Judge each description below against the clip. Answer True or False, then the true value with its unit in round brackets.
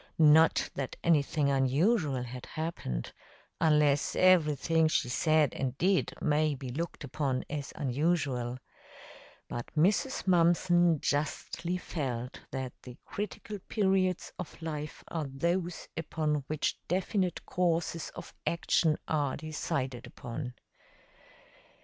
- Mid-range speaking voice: True (155 Hz)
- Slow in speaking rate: True (110 wpm)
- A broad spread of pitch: False (3.8 semitones)